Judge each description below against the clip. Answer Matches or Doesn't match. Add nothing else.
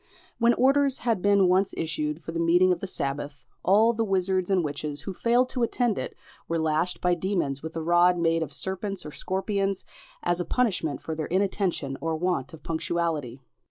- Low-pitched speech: Doesn't match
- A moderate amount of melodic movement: Matches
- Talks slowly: Doesn't match